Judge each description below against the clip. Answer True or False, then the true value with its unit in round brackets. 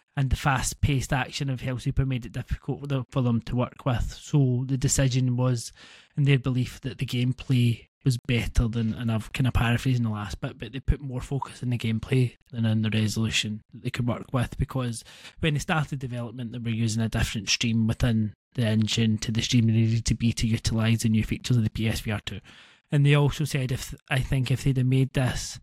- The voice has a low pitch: True (125 Hz)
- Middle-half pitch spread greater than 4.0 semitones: False (2.9 semitones)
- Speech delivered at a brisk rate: True (225 wpm)